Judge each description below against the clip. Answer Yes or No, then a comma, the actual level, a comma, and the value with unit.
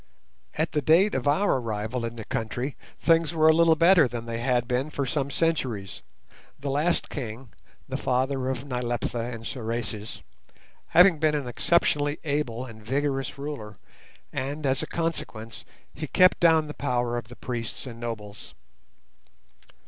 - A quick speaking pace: No, average, 155 wpm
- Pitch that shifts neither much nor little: Yes, average, 4.4 semitones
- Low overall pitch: Yes, low, 130 Hz